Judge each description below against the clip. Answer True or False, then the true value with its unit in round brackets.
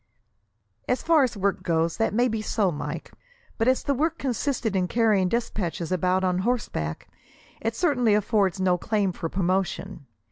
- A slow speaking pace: False (165 wpm)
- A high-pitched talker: True (205 Hz)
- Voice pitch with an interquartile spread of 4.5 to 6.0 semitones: True (4.8 semitones)